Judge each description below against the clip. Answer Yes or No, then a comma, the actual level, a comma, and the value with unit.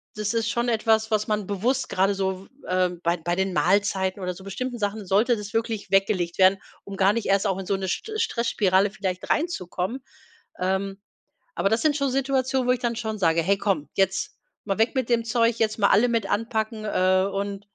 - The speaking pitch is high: Yes, high, 205 Hz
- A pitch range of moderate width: Yes, average, 3.2 semitones